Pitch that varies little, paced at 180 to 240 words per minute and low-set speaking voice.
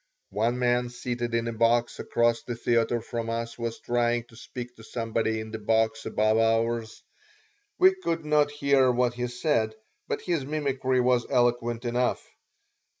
No: narrow, 1.5 semitones; average, 160 wpm; low, 120 Hz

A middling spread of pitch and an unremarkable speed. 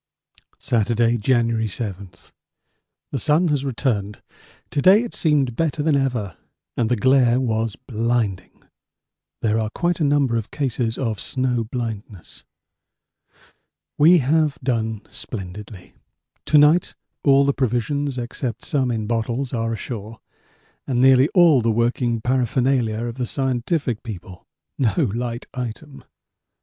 No: average, 3.5 semitones; slow, 130 wpm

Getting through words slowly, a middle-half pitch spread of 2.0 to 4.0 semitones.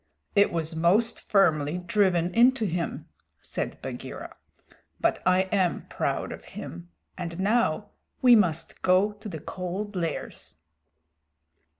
Yes: slow, 120 wpm; average, 3.7 semitones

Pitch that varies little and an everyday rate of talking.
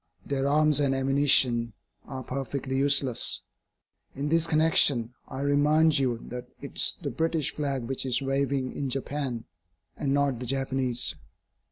Yes: narrow, 1.8 semitones; average, 145 wpm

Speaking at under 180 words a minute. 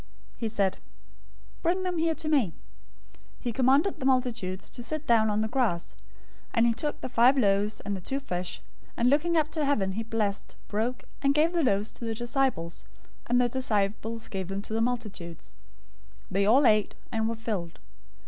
No: average, 190 wpm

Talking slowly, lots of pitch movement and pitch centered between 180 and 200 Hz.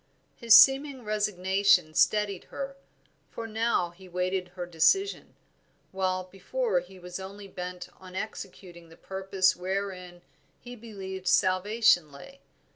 No: slow, 120 wpm; average, 3.0 semitones; high, 190 Hz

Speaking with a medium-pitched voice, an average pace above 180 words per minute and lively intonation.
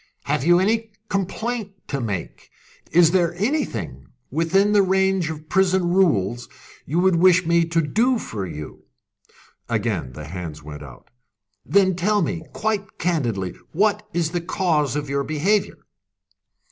No: medium, 170 Hz; average, 145 wpm; wide, 6.7 semitones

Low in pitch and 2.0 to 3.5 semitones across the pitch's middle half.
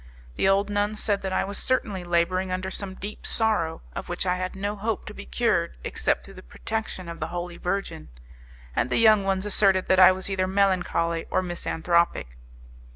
No: high, 190 Hz; narrow, 2.5 semitones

